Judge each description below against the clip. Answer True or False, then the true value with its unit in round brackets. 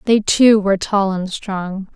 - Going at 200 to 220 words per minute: False (185 wpm)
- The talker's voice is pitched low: False (200 Hz)